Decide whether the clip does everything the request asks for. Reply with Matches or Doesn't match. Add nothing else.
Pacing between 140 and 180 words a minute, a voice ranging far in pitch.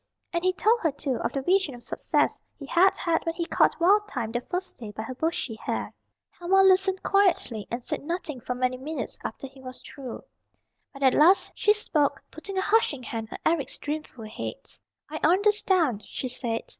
Doesn't match